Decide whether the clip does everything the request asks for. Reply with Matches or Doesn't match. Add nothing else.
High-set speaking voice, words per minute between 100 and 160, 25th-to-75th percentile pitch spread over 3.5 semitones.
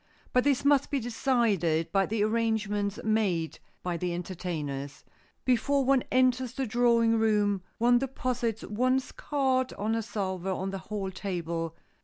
Matches